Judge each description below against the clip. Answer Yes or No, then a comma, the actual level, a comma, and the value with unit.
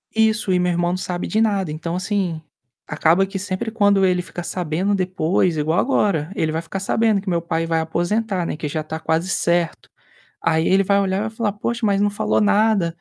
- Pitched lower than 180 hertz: No, medium, 185 Hz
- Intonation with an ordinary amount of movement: Yes, average, 3.5 semitones